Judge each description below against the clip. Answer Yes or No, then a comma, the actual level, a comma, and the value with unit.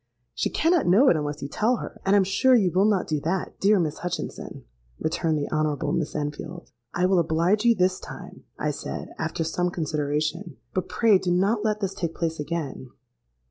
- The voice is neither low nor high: Yes, medium, 175 Hz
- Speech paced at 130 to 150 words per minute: No, average, 195 wpm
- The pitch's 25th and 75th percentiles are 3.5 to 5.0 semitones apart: Yes, average, 4.1 semitones